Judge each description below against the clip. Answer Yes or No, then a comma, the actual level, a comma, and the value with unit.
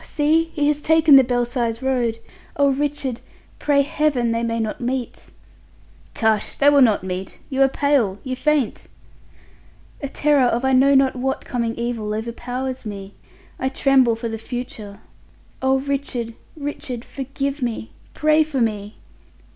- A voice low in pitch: No, very high, 255 Hz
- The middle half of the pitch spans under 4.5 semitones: Yes, average, 3.4 semitones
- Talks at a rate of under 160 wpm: Yes, average, 150 wpm